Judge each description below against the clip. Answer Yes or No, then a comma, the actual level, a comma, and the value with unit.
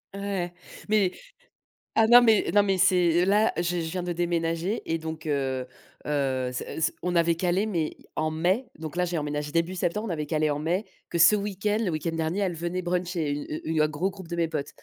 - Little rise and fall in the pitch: No, average, 3.1 semitones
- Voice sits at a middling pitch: Yes, medium, 170 Hz